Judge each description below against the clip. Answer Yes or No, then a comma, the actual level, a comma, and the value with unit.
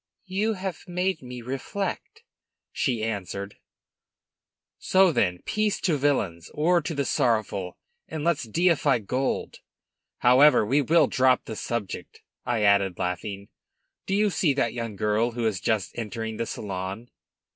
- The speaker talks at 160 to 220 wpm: No, average, 140 wpm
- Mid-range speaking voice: No, low, 120 Hz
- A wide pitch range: Yes, wide, 7.5 semitones